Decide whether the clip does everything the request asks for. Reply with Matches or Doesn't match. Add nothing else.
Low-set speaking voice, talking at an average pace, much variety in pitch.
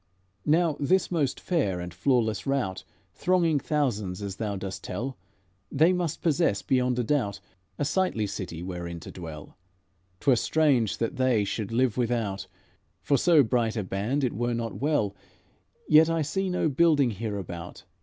Matches